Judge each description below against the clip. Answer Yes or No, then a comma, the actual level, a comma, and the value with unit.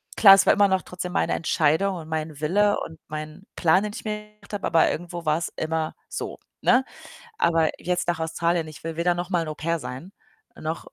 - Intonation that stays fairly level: No, average, 3.3 semitones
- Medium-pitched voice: Yes, medium, 170 Hz